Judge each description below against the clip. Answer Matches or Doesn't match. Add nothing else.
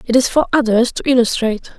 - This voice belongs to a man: Doesn't match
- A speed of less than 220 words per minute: Matches